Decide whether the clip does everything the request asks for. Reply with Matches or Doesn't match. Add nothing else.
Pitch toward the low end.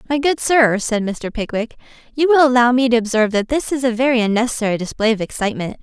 Doesn't match